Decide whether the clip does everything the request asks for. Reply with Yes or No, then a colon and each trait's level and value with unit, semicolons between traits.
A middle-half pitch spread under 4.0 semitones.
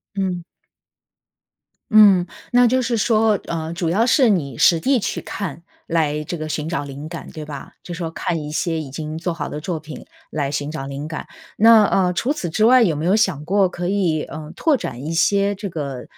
No: average, 4.8 semitones